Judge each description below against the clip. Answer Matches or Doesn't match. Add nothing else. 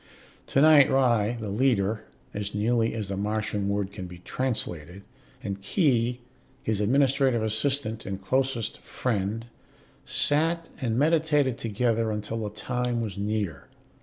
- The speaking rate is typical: Doesn't match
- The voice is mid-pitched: Doesn't match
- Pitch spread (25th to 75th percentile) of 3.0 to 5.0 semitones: Matches